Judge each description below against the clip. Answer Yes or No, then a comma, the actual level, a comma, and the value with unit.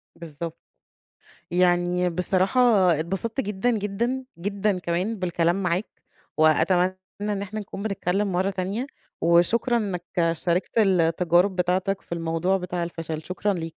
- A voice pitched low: No, medium, 185 Hz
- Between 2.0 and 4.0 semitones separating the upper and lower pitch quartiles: Yes, average, 2.7 semitones